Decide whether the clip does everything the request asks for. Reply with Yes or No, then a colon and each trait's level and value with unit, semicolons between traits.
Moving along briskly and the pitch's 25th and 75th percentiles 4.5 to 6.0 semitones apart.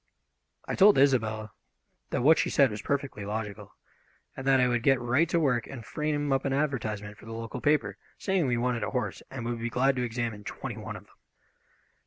No: fast, 210 wpm; average, 3.7 semitones